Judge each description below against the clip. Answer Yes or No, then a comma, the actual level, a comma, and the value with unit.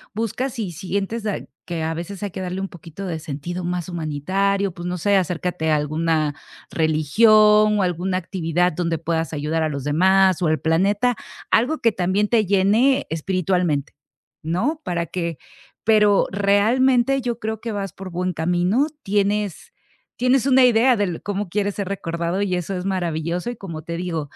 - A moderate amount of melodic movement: Yes, average, 3.8 semitones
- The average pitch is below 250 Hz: Yes, medium, 185 Hz